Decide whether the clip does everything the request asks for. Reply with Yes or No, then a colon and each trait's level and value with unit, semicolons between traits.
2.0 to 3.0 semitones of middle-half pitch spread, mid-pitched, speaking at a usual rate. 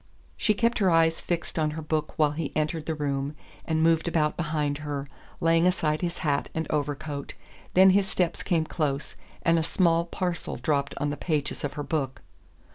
Yes: narrow, 2.4 semitones; medium, 160 Hz; average, 190 wpm